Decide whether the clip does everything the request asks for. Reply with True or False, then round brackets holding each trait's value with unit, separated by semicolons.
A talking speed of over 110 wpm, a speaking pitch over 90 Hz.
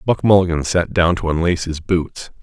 False (200 wpm; 85 Hz)